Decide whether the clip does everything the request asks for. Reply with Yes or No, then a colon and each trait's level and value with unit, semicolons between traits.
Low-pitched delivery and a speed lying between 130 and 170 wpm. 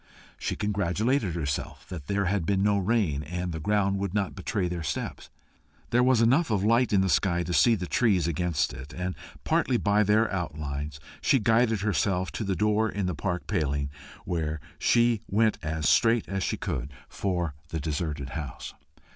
No: very low, 95 Hz; average, 180 wpm